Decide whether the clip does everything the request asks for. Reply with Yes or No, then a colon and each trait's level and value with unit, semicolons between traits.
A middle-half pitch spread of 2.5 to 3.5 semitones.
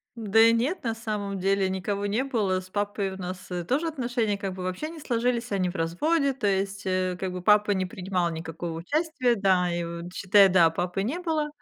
No: average, 4.3 semitones